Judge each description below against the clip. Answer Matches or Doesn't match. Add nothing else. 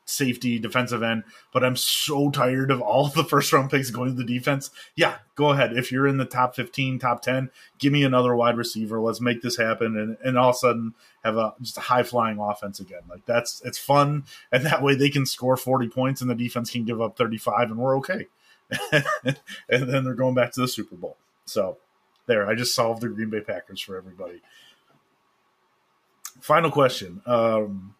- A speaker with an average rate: Doesn't match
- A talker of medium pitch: Doesn't match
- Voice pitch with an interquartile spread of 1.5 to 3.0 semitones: Matches